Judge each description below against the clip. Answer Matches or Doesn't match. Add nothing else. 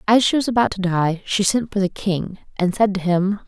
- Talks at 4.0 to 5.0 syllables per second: Doesn't match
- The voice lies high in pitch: Matches